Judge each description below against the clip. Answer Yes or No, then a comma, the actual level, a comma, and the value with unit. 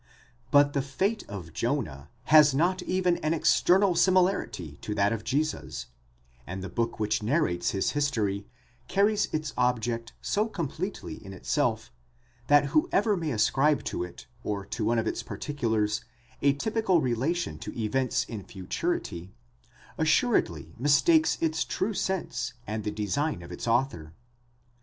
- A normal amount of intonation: No, wide, 7.9 semitones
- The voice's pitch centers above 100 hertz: Yes, low, 135 Hz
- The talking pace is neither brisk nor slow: Yes, average, 145 wpm